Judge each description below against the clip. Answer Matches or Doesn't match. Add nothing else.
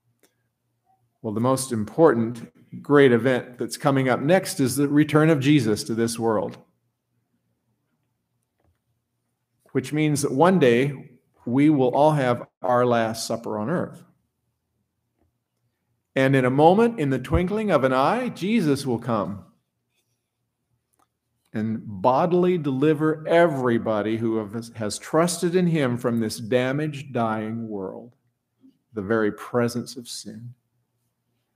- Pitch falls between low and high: Doesn't match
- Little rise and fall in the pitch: Doesn't match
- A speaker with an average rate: Doesn't match